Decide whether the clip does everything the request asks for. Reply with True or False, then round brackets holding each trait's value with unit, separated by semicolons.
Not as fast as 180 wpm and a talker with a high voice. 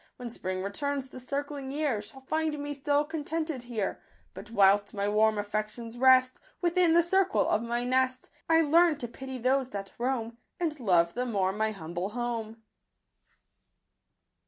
True (160 wpm; 250 Hz)